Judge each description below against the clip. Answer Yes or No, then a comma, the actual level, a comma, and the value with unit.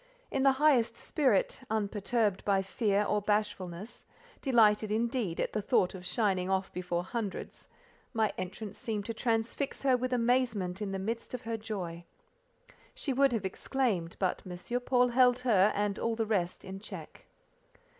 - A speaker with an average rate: Yes, average, 155 wpm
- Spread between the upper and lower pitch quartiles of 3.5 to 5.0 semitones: Yes, average, 4.1 semitones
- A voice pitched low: No, high, 215 Hz